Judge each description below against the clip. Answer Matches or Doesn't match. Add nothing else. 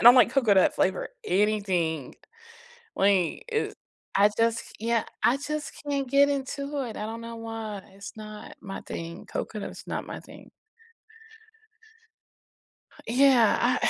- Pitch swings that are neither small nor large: Matches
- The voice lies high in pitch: Matches